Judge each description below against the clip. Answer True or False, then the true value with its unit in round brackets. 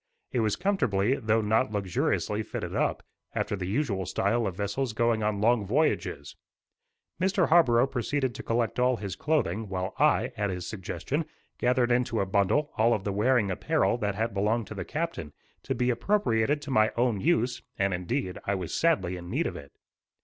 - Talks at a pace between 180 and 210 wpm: True (185 wpm)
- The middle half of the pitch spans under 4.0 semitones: False (4.4 semitones)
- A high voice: False (110 Hz)